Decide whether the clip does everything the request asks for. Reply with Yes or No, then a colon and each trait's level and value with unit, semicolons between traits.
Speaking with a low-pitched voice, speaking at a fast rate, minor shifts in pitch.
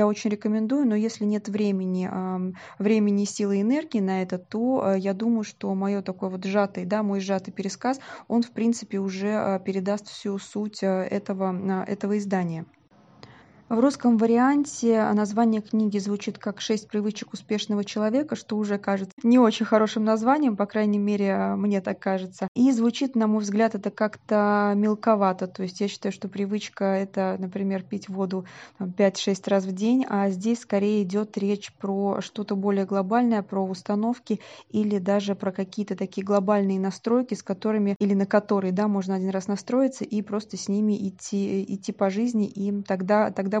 No: high, 205 Hz; fast, 165 wpm; narrow, 1.8 semitones